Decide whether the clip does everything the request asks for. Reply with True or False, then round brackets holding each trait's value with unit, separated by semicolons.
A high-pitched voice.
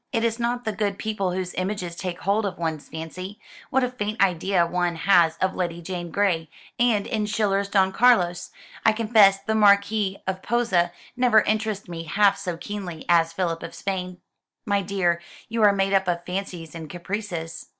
True (195 Hz)